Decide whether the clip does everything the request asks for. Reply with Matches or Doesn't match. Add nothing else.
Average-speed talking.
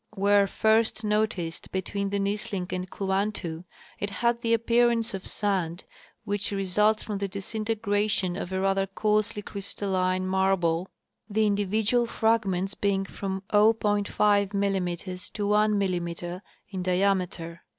Doesn't match